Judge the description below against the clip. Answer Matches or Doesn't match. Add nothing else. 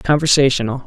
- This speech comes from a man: Matches